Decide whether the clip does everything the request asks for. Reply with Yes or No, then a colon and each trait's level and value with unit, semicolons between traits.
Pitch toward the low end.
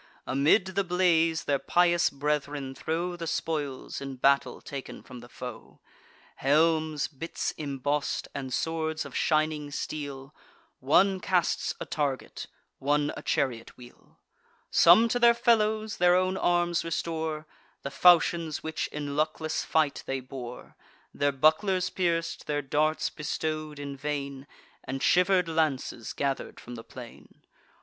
No: medium, 155 Hz